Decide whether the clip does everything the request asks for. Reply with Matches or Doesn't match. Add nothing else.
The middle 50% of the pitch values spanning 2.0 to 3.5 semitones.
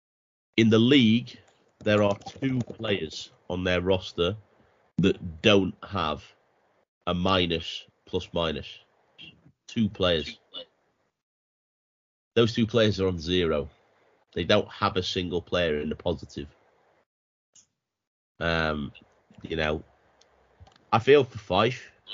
Doesn't match